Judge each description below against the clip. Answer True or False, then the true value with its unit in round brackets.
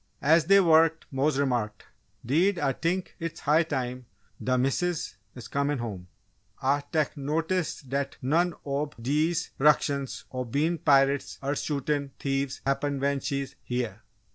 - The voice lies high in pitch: False (140 Hz)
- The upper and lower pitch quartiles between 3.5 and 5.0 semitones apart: False (3.0 semitones)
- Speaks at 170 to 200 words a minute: False (140 wpm)